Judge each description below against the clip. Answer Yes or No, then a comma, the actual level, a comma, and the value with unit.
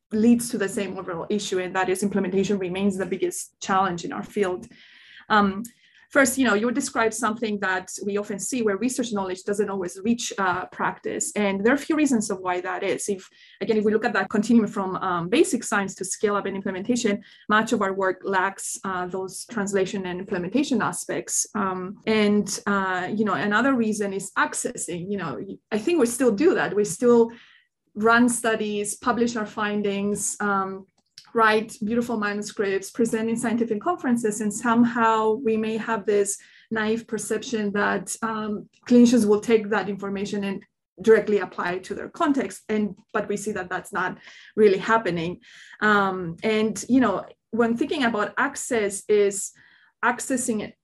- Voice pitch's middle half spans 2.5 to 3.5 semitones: Yes, average, 2.8 semitones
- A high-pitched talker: Yes, high, 210 Hz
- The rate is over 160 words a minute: Yes, average, 175 wpm